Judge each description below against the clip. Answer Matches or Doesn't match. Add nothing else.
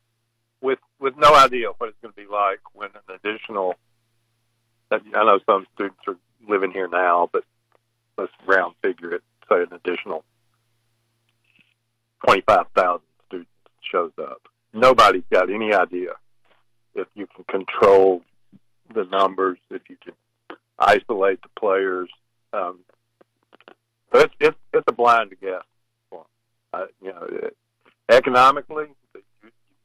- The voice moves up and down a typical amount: Doesn't match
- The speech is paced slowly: Matches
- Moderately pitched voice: Doesn't match